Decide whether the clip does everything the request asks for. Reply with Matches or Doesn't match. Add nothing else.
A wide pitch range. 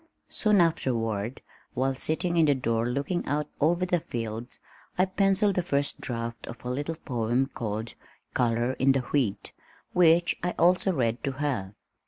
Matches